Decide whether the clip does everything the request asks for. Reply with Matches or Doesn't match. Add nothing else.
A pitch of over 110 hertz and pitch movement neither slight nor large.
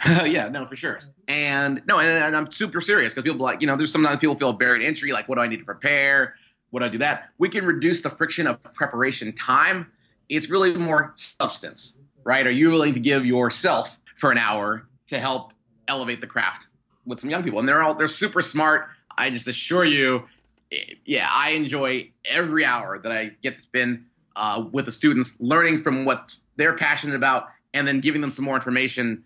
Matches